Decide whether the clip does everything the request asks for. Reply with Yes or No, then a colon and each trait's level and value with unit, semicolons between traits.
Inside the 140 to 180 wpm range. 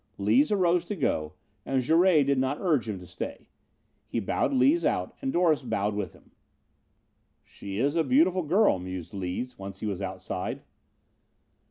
Yes: average, 165 wpm